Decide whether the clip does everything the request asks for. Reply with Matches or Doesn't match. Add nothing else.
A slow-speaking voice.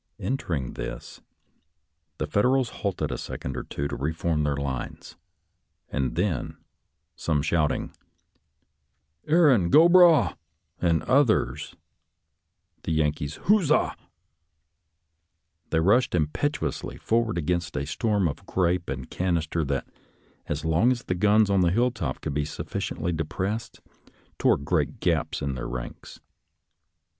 Matches